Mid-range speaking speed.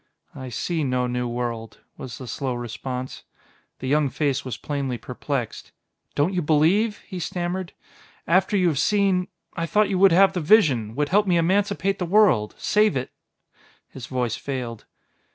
Yes: average, 170 wpm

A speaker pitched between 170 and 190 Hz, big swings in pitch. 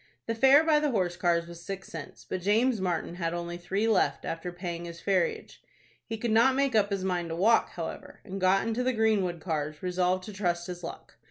No: medium, 185 Hz; average, 4.3 semitones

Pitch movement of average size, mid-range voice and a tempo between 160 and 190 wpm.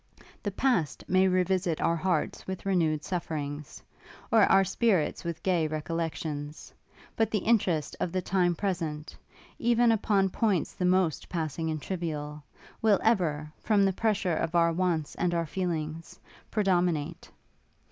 No: average, 3.4 semitones; medium, 175 Hz; average, 145 wpm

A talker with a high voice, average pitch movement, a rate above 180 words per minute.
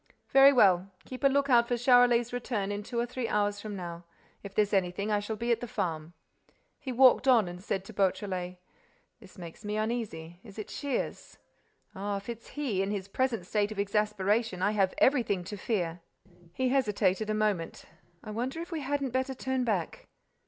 Yes: high, 210 Hz; average, 4.1 semitones; average, 190 wpm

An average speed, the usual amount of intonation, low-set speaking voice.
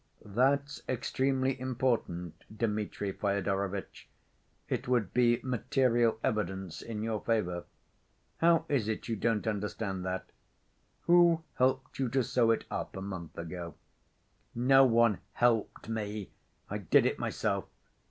No: slow, 125 wpm; average, 4.4 semitones; low, 115 Hz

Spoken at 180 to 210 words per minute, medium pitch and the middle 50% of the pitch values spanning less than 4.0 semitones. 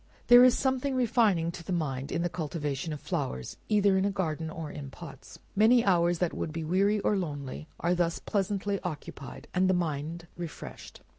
No: average, 190 wpm; medium, 175 Hz; average, 4.4 semitones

